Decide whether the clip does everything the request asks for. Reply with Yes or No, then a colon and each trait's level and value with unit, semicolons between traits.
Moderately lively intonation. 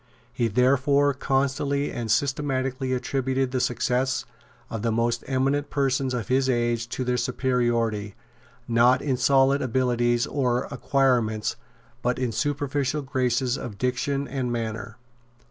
No: narrow, 2.1 semitones